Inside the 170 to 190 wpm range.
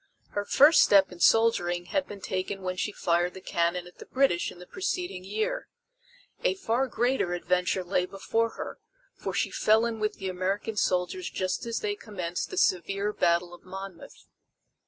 Yes: average, 175 wpm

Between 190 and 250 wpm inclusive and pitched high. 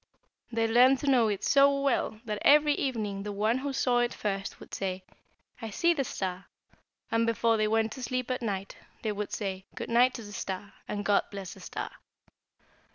Yes: average, 200 wpm; high, 225 Hz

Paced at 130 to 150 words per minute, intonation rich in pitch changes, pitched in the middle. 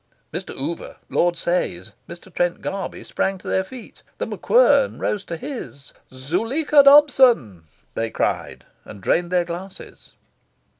Yes: slow, 135 wpm; wide, 7.1 semitones; medium, 180 Hz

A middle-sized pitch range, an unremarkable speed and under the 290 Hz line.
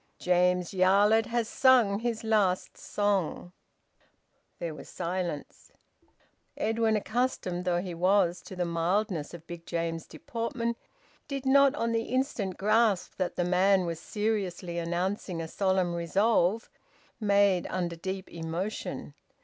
No: average, 4.0 semitones; slow, 125 wpm; high, 190 Hz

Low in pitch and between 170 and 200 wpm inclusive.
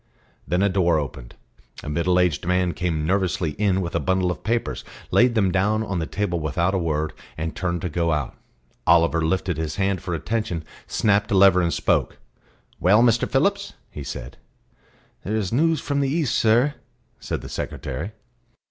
Yes: very low, 90 Hz; average, 180 wpm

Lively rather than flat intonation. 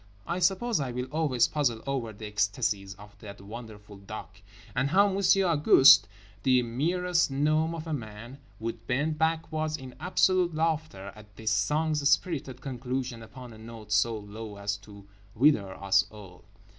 Yes: wide, 6.7 semitones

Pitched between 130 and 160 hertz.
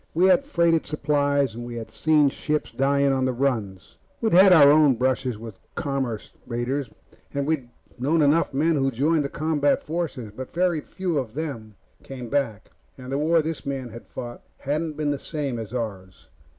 Yes: medium, 140 Hz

